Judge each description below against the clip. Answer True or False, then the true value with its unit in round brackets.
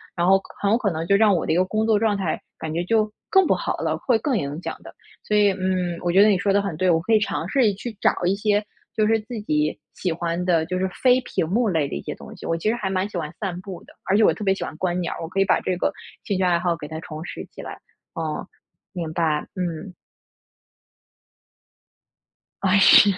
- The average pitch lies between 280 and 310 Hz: False (185 Hz)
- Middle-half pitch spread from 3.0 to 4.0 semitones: True (3.7 semitones)